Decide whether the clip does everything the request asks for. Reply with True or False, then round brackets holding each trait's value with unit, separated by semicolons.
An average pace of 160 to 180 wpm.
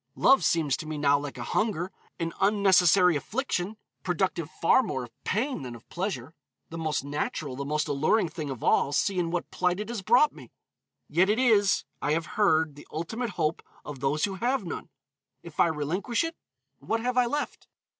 False (190 wpm)